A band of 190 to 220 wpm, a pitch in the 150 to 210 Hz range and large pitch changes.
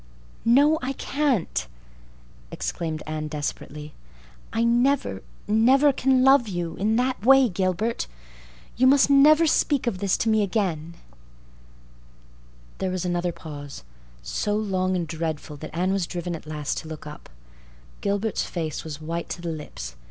No: average, 140 wpm; medium, 185 Hz; wide, 7.3 semitones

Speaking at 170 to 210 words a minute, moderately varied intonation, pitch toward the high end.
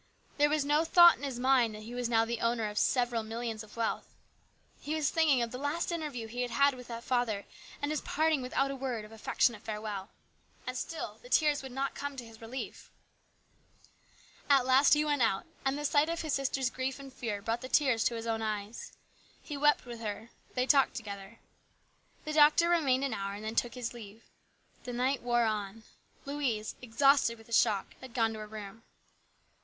Yes: fast, 205 wpm; average, 3.8 semitones; high, 245 Hz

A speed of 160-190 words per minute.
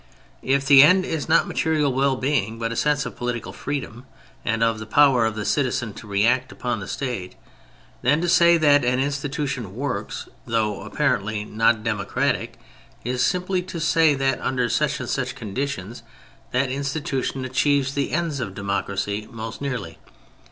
Yes: average, 170 wpm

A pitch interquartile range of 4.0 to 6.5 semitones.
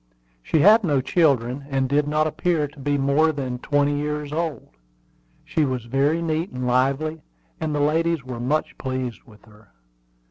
No: average, 3.2 semitones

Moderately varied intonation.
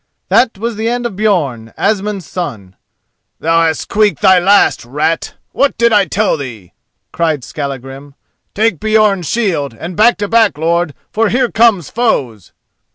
No: wide, 7.0 semitones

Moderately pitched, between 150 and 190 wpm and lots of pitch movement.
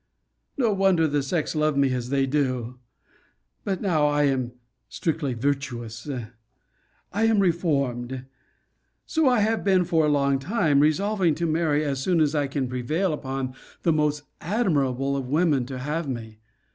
No: medium, 145 Hz; average, 160 wpm; average, 4.3 semitones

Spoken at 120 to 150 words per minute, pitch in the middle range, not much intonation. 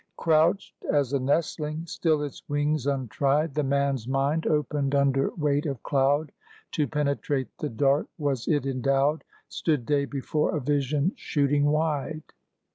Yes: average, 140 wpm; medium, 145 Hz; narrow, 1.8 semitones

